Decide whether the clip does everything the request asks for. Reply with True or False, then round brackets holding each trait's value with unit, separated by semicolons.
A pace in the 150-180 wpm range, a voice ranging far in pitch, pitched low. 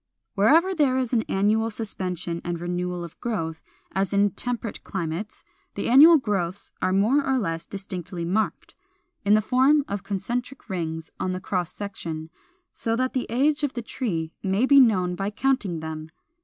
False (170 wpm; 5.8 semitones; 200 Hz)